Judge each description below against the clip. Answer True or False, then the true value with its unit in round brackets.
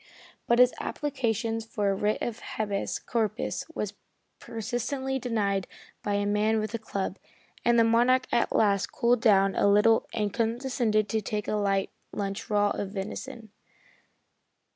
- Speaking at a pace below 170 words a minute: True (150 wpm)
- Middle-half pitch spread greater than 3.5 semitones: False (2.6 semitones)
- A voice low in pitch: False (220 Hz)